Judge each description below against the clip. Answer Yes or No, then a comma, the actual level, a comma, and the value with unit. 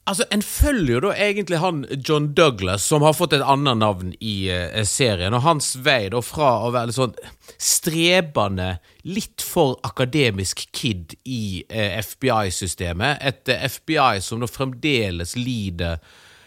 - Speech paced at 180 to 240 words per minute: No, average, 155 wpm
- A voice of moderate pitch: No, low, 120 Hz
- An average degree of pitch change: No, wide, 6.9 semitones